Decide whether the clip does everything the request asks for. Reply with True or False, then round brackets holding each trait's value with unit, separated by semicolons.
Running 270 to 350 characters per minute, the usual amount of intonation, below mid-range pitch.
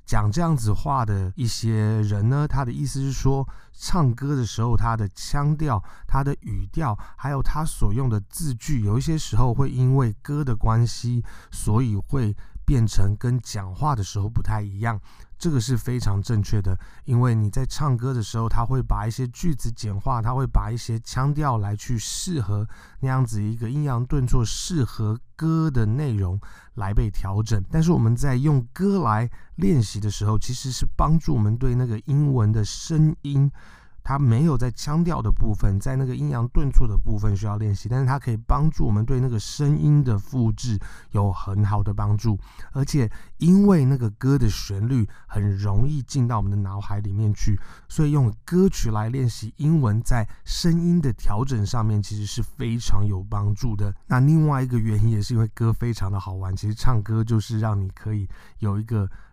True (275 characters per minute; 4.3 semitones; 115 Hz)